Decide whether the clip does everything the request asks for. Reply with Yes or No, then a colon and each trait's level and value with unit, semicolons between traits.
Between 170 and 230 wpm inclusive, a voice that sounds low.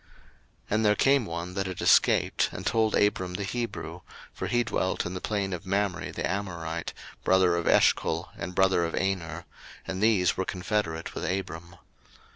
Yes: average, 175 wpm; very low, 95 Hz